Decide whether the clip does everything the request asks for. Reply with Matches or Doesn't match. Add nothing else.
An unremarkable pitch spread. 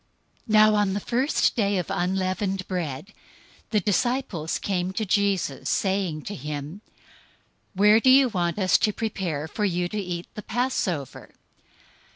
Matches